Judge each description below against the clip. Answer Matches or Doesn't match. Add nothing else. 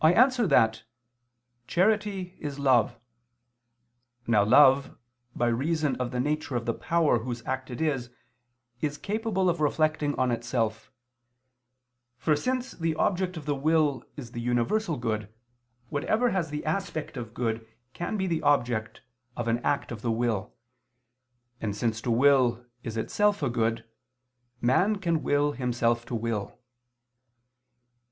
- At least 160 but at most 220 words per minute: Doesn't match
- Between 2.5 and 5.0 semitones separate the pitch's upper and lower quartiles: Doesn't match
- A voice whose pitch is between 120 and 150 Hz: Matches